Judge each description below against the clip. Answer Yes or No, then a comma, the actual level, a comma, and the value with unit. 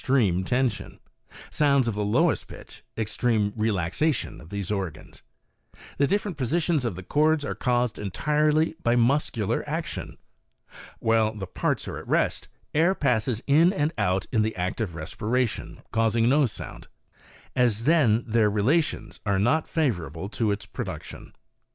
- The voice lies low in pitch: Yes, low, 115 Hz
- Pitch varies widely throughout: Yes, wide, 5.8 semitones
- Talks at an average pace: Yes, average, 150 wpm